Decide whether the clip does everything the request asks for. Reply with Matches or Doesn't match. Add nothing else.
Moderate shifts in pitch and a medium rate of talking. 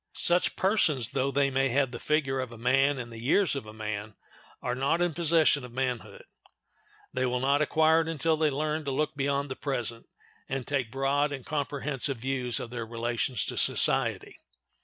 Matches